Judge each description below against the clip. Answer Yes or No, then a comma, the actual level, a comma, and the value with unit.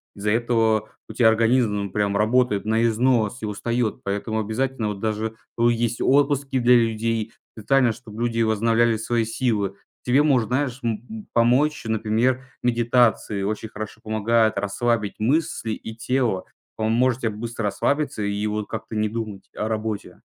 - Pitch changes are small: Yes, narrow, 2.2 semitones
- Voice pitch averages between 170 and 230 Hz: No, low, 115 Hz